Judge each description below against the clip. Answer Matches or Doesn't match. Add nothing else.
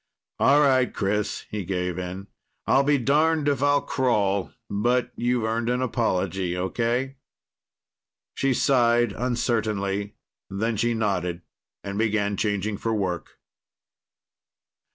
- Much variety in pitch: Doesn't match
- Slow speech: Matches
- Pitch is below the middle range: Matches